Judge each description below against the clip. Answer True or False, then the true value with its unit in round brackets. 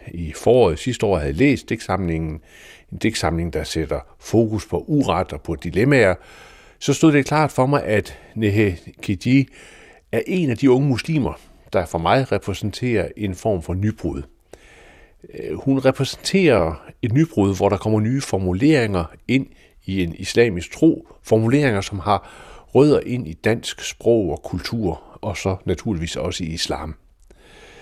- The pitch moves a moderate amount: False (6.7 semitones)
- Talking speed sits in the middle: True (155 wpm)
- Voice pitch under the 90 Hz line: False (105 Hz)